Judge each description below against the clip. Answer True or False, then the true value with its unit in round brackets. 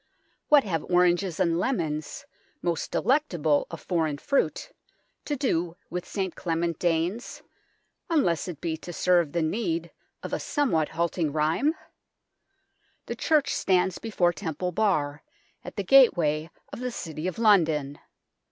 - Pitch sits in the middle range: True (175 Hz)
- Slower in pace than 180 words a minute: True (135 wpm)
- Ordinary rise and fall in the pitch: True (4.3 semitones)